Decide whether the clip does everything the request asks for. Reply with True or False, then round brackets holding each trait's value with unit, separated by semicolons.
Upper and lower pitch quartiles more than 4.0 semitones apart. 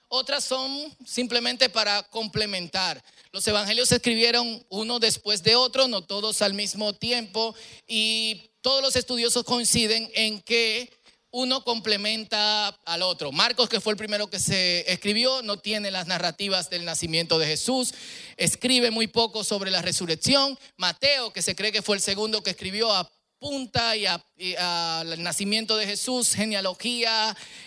False (3.6 semitones)